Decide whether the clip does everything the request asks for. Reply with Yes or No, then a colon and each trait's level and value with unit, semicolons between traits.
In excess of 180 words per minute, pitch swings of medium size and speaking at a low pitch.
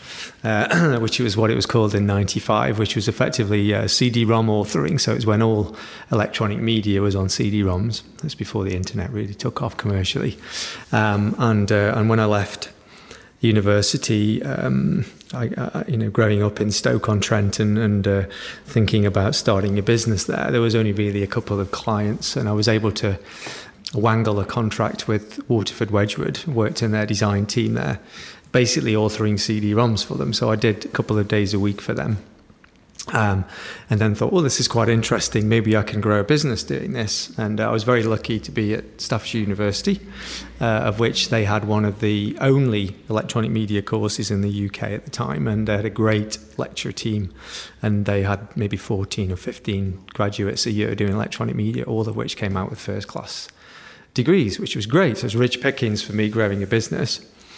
No: average, 195 wpm; narrow, 1.7 semitones; low, 110 Hz